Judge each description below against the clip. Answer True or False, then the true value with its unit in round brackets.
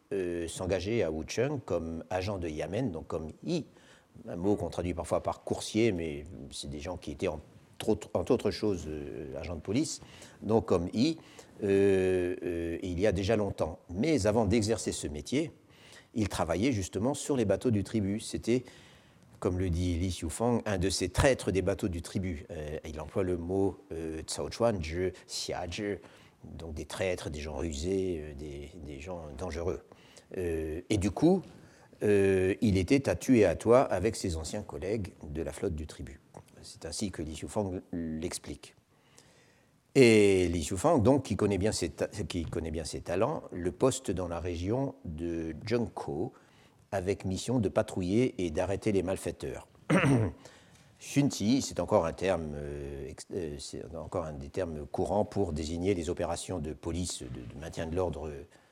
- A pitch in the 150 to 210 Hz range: False (95 Hz)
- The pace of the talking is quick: False (170 wpm)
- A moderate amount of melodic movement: True (4.0 semitones)